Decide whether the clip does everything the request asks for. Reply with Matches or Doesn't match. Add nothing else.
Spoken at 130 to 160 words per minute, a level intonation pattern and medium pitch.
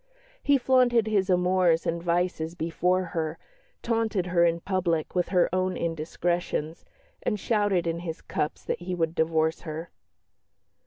Matches